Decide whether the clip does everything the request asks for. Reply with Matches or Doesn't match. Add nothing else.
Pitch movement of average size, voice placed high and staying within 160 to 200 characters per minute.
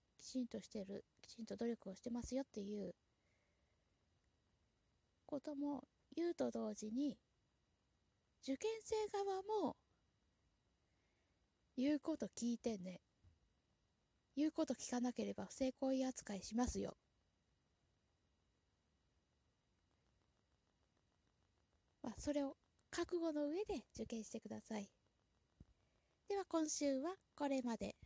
Doesn't match